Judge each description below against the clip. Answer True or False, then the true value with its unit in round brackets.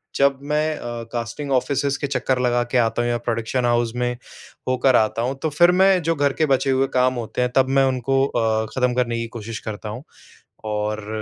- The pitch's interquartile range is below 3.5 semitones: True (2.7 semitones)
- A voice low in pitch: True (125 Hz)